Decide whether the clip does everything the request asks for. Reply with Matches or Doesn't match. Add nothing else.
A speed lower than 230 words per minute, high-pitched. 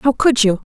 Doesn't match